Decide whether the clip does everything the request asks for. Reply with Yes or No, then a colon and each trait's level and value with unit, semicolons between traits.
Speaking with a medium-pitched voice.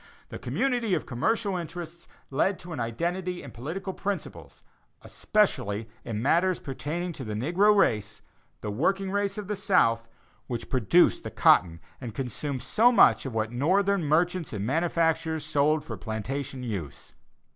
Yes: medium, 155 Hz